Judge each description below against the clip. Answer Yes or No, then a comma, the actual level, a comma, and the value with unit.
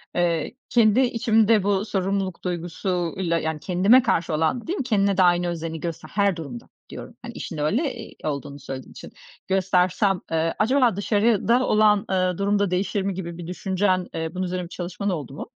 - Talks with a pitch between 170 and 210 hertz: Yes, medium, 185 Hz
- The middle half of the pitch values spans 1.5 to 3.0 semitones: No, average, 3.4 semitones